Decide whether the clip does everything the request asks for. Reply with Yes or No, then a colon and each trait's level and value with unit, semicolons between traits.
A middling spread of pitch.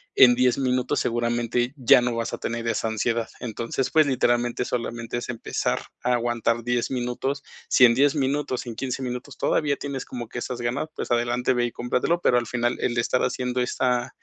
No: narrow, 1.3 semitones